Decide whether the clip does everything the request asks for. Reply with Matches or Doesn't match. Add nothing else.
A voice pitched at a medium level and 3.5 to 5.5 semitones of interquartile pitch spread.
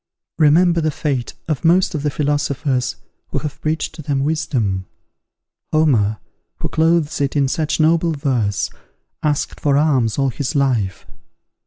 Doesn't match